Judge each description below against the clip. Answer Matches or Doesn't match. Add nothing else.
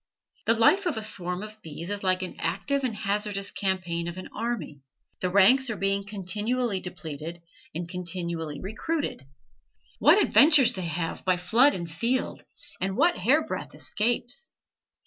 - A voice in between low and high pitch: Doesn't match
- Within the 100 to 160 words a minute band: Matches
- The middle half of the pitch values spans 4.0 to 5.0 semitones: Matches